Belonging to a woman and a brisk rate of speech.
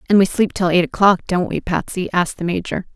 Yes: female; fast, 245 wpm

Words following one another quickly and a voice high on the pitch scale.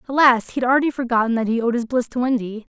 Yes: fast, 265 wpm; high, 240 Hz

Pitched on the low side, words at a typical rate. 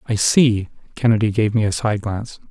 Yes: low, 110 Hz; average, 190 wpm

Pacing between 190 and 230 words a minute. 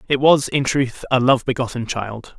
Yes: average, 200 wpm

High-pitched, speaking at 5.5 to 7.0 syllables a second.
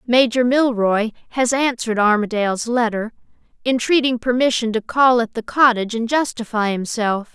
No: high, 235 Hz; 5.1 syllables/s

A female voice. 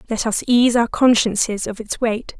Yes: female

